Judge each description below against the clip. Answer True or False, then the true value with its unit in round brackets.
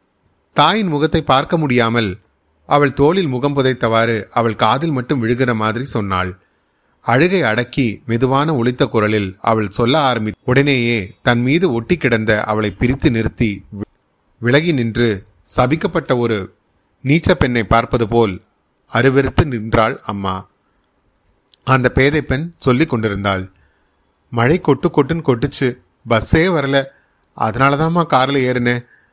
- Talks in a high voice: False (120 Hz)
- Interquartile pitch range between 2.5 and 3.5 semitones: False (4.3 semitones)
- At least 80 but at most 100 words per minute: False (110 wpm)